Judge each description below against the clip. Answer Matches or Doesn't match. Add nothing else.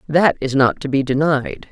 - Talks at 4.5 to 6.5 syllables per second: Matches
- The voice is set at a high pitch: Doesn't match